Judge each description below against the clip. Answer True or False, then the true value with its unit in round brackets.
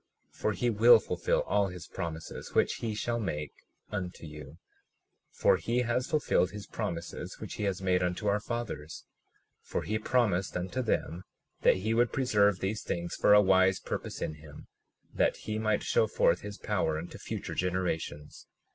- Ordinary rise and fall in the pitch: True (3.7 semitones)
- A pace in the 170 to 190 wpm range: True (175 wpm)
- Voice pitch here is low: True (95 Hz)